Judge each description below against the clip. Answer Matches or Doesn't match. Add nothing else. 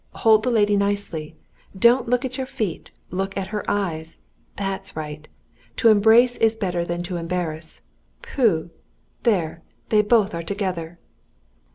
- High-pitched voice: Matches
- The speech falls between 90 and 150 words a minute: Matches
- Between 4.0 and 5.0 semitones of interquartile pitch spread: Matches